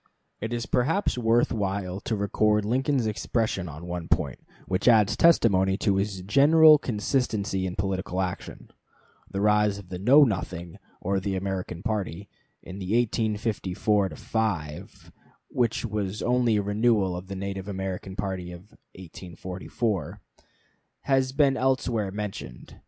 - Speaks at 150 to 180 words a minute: No, slow, 135 wpm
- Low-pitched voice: Yes, low, 100 Hz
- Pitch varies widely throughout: No, average, 3.5 semitones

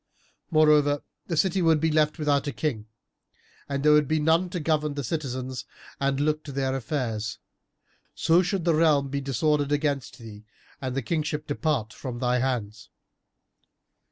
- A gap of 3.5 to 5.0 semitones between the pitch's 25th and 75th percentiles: No, average, 3.0 semitones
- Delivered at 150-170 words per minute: Yes, average, 155 wpm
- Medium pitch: Yes, medium, 145 Hz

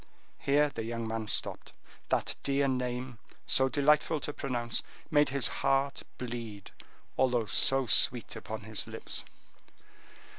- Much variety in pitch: No, average, 3.1 semitones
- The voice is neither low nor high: No, low, 125 Hz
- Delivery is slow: Yes, slow, 125 wpm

